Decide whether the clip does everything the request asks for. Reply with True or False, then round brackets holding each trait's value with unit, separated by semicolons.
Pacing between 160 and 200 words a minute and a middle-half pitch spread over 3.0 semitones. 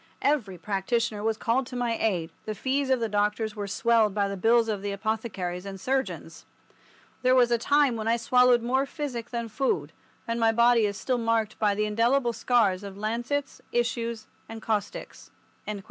False (180 wpm; 2.6 semitones)